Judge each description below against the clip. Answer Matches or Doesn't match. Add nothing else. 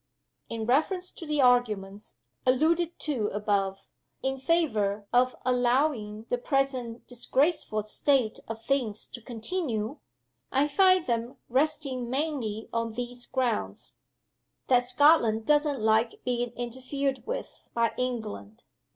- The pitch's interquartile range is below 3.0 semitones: Doesn't match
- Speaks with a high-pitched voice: Matches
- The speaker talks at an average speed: Doesn't match